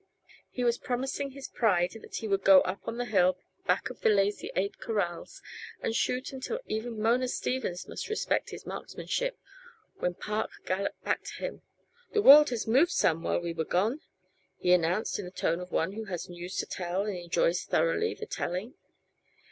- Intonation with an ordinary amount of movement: No, wide, 5.9 semitones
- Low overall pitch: No, high, 210 Hz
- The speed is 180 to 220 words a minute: Yes, average, 190 wpm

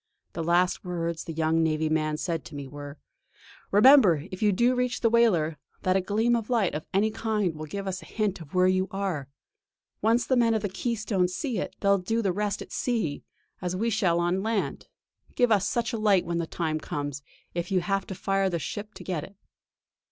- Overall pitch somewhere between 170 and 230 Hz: Yes, high, 190 Hz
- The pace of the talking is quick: Yes, fast, 220 wpm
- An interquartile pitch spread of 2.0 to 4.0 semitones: No, average, 4.5 semitones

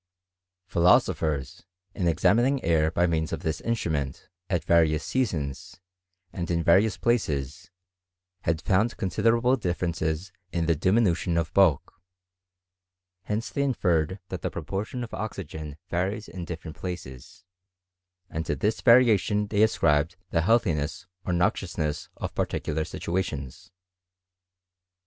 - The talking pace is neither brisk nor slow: No, slow, 125 wpm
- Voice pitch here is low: Yes, very low, 85 Hz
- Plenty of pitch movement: No, average, 4.7 semitones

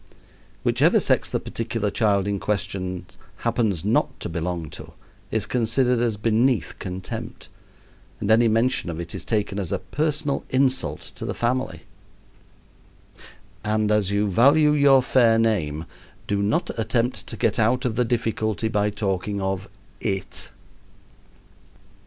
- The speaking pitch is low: Yes, low, 110 Hz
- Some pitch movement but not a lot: Yes, average, 3.5 semitones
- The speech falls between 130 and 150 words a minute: Yes, average, 140 wpm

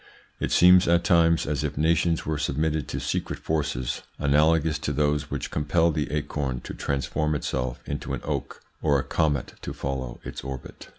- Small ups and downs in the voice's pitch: Yes, narrow, 2.3 semitones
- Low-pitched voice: Yes, very low, 75 Hz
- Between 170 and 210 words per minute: Yes, average, 175 wpm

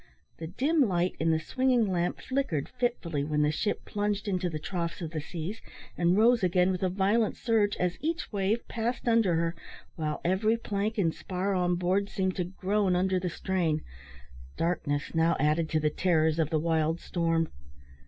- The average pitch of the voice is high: No, medium, 180 Hz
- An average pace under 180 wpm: No, average, 185 wpm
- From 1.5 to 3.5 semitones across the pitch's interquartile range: No, average, 3.9 semitones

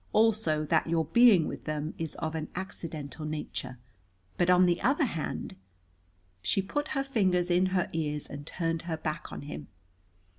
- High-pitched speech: No, medium, 165 Hz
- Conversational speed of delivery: Yes, average, 175 wpm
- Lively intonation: No, average, 3.6 semitones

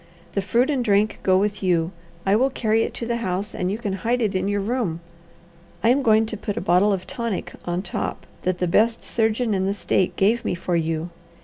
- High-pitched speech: Yes, high, 205 Hz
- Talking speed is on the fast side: Yes, fast, 230 wpm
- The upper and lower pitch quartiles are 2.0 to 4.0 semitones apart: Yes, average, 3.6 semitones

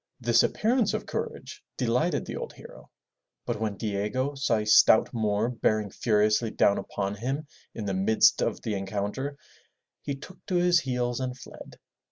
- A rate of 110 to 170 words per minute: Yes, average, 165 wpm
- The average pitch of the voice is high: No, low, 115 Hz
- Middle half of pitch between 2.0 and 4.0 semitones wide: No, average, 4.8 semitones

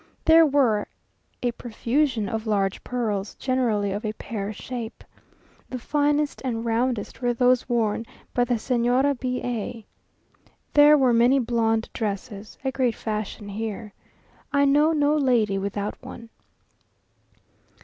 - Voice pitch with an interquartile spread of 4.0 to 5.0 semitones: No, average, 3.3 semitones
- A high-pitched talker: Yes, high, 235 Hz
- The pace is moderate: No, slow, 130 wpm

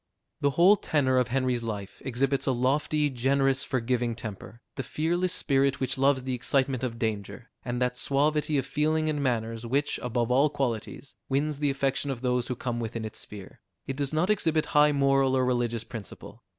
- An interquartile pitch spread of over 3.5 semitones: No, average, 2.8 semitones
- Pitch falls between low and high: No, low, 130 Hz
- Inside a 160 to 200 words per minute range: Yes, average, 185 wpm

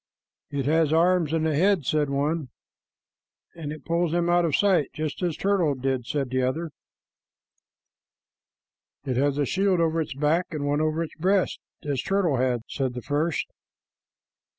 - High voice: No, medium, 155 Hz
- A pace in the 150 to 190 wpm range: Yes, average, 160 wpm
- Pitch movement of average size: Yes, average, 3.2 semitones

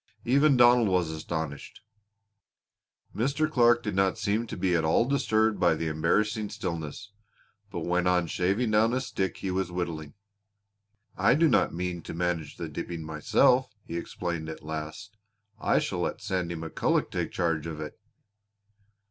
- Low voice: Yes, very low, 90 Hz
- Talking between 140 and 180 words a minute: Yes, average, 155 wpm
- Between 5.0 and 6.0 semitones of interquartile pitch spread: Yes, average, 5.3 semitones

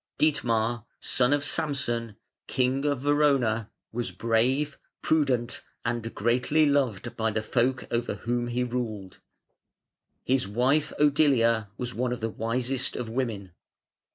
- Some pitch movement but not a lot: Yes, average, 3.0 semitones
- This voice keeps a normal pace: No, slow, 125 wpm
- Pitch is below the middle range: Yes, low, 125 Hz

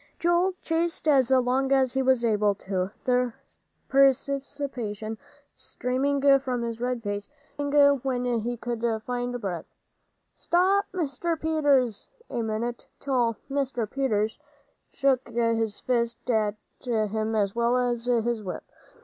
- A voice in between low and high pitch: No, high, 245 Hz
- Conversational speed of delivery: No, slow, 125 wpm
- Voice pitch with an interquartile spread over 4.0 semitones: No, average, 3.4 semitones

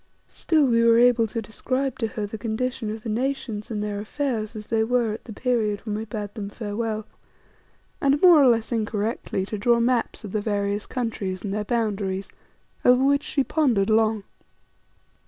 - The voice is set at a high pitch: Yes, high, 225 Hz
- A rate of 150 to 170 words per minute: No, average, 185 wpm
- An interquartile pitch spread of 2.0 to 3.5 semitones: Yes, average, 2.9 semitones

